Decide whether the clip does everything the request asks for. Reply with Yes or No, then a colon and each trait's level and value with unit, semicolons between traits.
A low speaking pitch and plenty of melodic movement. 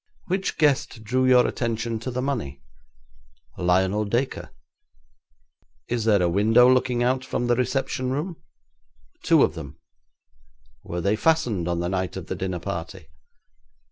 Yes: low, 115 Hz; wide, 5.7 semitones